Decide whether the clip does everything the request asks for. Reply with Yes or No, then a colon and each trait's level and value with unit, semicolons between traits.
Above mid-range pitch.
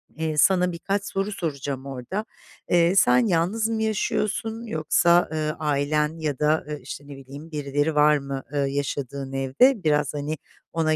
No: medium, 150 Hz